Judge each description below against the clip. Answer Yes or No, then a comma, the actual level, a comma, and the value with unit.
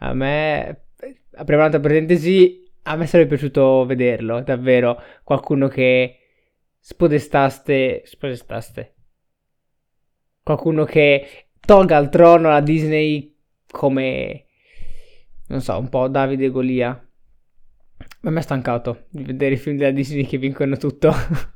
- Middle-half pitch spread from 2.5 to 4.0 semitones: Yes, average, 2.8 semitones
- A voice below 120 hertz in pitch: No, medium, 140 Hz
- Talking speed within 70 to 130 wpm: Yes, average, 120 wpm